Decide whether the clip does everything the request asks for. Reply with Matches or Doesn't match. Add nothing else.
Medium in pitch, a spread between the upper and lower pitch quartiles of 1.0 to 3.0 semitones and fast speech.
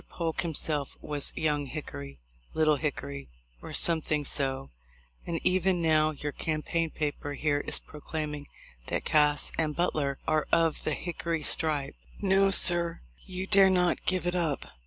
Doesn't match